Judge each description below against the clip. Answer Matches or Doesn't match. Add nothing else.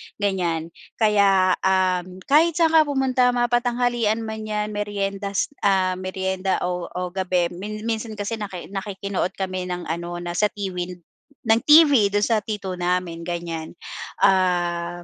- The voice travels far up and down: Doesn't match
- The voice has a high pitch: Matches